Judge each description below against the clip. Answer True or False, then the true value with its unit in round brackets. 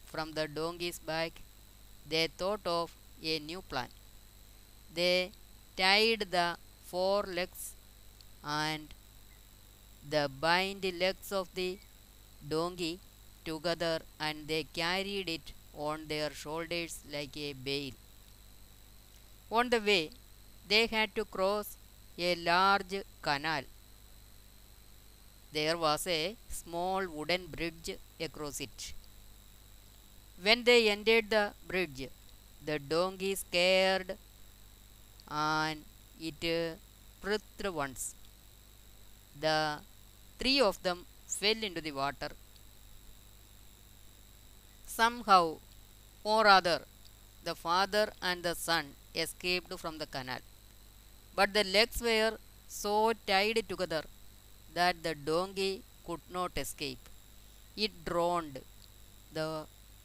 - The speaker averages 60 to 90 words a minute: False (100 wpm)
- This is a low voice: False (150 Hz)